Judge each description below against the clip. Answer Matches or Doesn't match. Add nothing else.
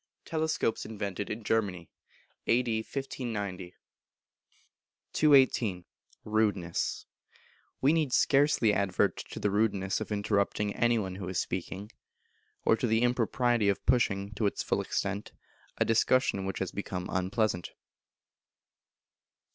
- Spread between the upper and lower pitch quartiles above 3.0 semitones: Matches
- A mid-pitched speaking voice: Doesn't match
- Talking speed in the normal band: Doesn't match